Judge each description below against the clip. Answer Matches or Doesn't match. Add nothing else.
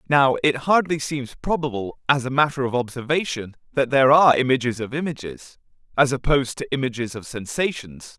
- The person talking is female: Doesn't match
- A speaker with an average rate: Matches